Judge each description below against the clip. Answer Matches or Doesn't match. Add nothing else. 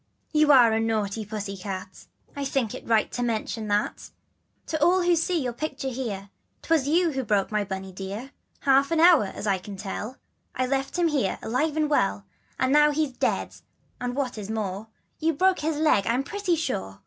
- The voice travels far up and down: Matches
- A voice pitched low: Doesn't match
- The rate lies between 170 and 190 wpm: Doesn't match